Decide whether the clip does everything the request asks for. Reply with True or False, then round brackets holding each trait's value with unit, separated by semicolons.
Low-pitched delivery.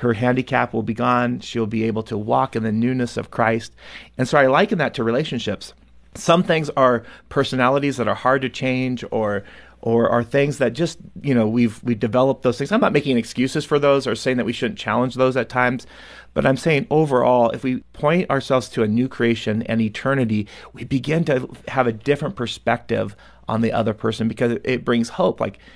True (125 Hz)